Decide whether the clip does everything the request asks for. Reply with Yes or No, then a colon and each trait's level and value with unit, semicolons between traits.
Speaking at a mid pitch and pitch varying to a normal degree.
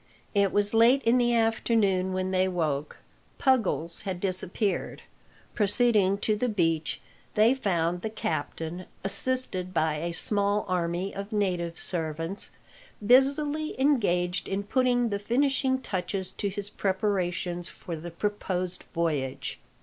No: high, 195 Hz; average, 4.2 semitones